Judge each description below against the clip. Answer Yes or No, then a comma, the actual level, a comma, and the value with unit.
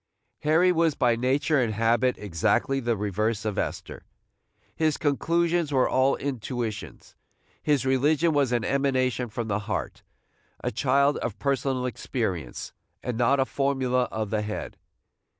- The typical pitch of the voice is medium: No, low, 130 Hz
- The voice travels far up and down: No, average, 3.8 semitones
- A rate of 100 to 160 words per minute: Yes, average, 140 wpm